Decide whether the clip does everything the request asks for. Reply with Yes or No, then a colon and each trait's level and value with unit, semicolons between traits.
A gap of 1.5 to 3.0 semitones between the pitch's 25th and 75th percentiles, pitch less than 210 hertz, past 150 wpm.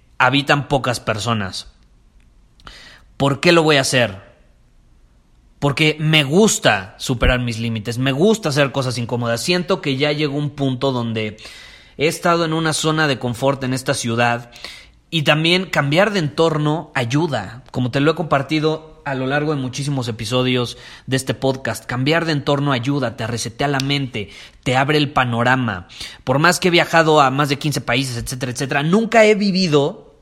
No: average, 4.3 semitones; medium, 140 Hz; average, 165 wpm